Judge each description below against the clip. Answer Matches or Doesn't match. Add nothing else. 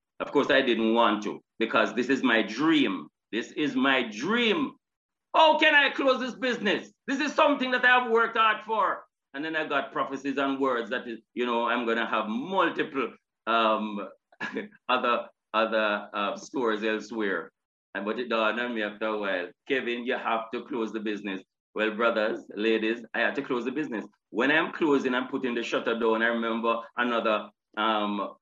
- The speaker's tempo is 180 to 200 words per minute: Matches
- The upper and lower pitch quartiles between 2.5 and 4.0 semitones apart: Doesn't match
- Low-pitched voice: Matches